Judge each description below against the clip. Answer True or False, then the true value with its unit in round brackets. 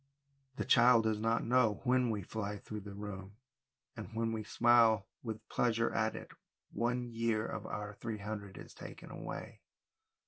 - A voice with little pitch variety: True (1.9 semitones)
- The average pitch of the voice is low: True (110 Hz)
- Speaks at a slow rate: False (165 wpm)